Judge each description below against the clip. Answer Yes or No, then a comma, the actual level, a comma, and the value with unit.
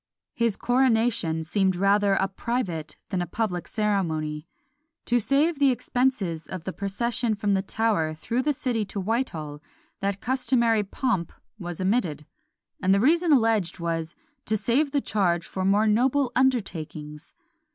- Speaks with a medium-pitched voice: No, high, 205 Hz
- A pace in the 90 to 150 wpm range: Yes, average, 145 wpm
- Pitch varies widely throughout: Yes, wide, 5.7 semitones